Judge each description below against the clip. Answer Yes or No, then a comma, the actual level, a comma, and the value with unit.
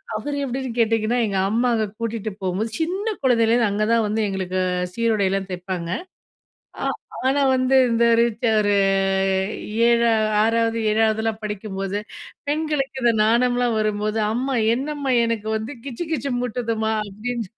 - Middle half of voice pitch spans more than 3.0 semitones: No, average, 2.7 semitones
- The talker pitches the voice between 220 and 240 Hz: Yes, high, 230 Hz